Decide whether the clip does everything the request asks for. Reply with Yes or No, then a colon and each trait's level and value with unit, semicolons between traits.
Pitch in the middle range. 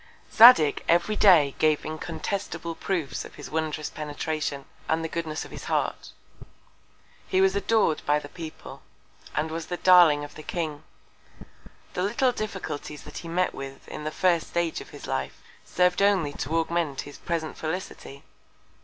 Yes: medium, 160 Hz